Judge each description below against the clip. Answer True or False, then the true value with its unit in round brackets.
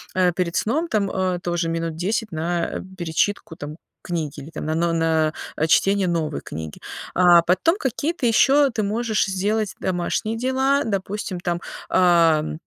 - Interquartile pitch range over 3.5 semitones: True (4.6 semitones)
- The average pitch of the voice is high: False (180 Hz)